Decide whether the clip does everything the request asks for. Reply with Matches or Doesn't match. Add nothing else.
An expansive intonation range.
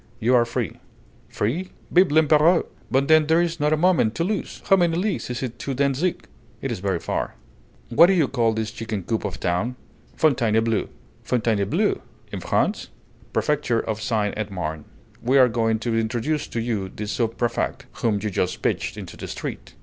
Matches